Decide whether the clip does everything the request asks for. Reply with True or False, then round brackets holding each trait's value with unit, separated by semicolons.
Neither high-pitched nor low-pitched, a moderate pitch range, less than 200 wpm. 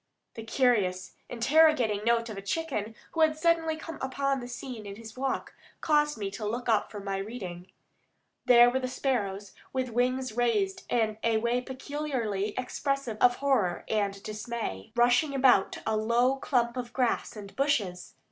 False (240 Hz; 4.0 semitones; 165 wpm)